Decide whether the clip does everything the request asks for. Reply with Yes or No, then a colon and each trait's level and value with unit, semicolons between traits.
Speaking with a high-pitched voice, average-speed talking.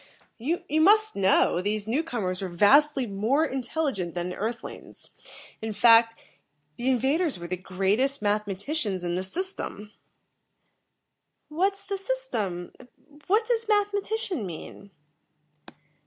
No: high, 235 Hz; slow, 120 wpm